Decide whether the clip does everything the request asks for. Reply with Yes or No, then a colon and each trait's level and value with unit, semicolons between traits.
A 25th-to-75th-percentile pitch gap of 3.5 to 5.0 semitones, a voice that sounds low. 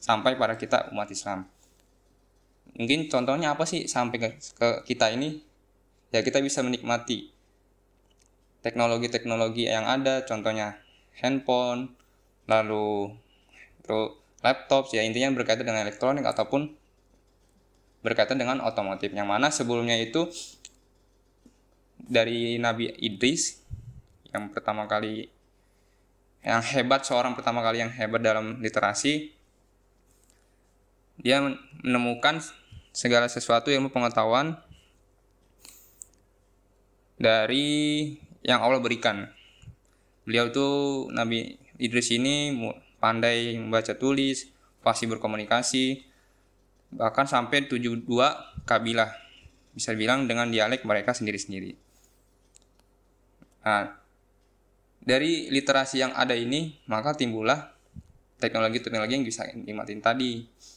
Yes: average, 4.2 semitones; low, 115 Hz